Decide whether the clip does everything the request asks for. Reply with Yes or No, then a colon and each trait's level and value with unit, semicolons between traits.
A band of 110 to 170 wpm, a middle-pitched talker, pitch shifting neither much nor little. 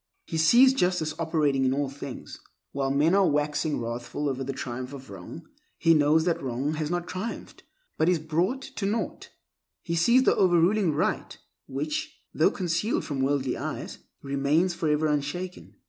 Yes: average, 160 wpm; medium, 155 Hz; average, 4.3 semitones